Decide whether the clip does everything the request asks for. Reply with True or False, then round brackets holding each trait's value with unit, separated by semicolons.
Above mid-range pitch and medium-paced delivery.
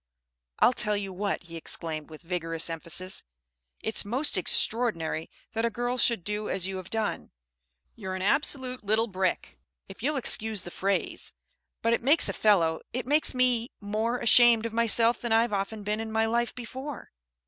True (220 Hz; 175 wpm)